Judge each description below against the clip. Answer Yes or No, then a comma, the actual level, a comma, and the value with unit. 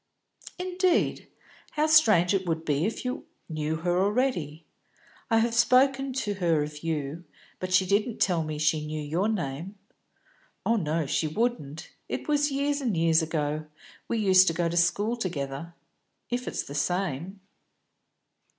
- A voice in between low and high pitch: Yes, medium, 180 Hz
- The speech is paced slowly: No, average, 155 wpm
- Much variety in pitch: Yes, wide, 6.8 semitones